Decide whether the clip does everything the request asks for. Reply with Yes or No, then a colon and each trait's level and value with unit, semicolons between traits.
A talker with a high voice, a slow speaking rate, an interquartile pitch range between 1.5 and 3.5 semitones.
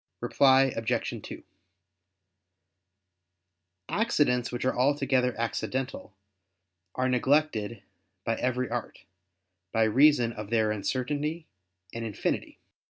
No: low, 125 Hz; slow, 95 wpm; average, 3.0 semitones